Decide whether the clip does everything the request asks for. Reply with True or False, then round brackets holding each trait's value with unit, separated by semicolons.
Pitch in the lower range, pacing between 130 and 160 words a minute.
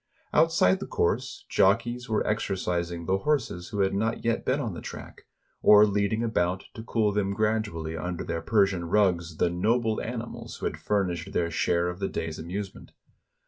False (100 Hz; 175 wpm)